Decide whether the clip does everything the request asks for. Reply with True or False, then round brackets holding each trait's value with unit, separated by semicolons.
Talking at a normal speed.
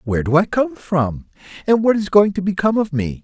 False (240 wpm)